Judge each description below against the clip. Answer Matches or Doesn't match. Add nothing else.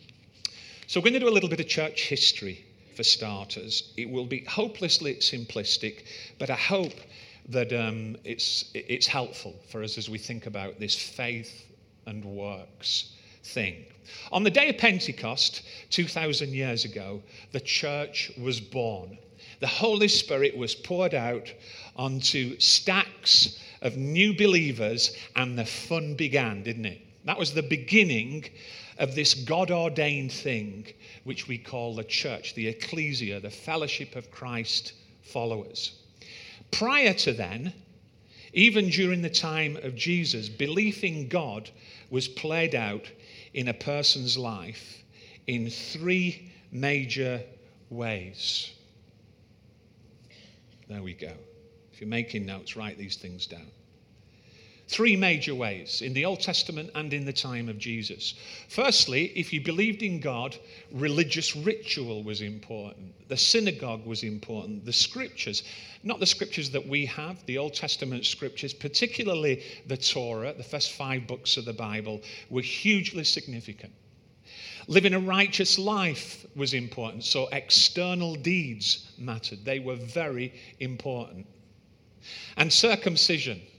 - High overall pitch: Doesn't match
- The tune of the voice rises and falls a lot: Matches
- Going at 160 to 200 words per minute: Doesn't match